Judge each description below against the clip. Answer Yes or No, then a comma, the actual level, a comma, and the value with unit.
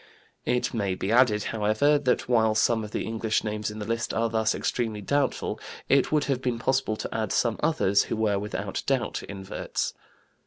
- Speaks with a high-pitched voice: No, low, 110 Hz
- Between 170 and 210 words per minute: Yes, average, 190 wpm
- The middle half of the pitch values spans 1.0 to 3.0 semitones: Yes, narrow, 2.6 semitones